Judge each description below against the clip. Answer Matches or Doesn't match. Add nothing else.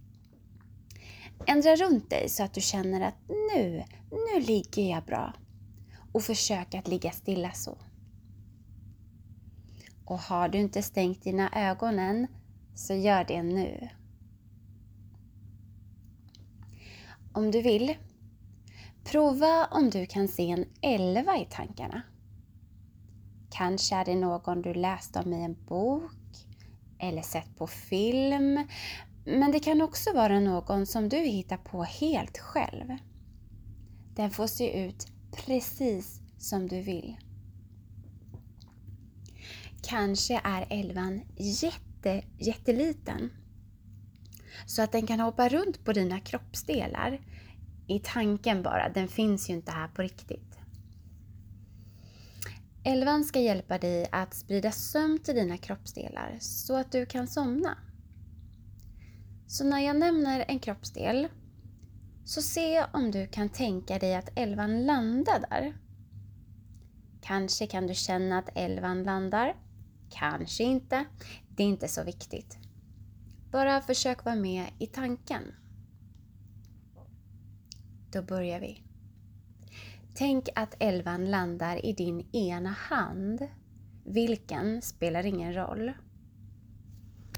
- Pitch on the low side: Doesn't match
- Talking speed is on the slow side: Matches